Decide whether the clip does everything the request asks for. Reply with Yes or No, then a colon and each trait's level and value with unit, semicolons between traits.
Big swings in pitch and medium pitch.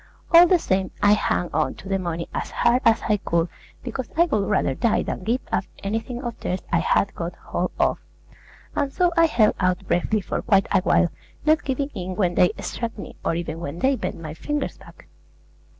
No: wide, 6.0 semitones; high, 200 Hz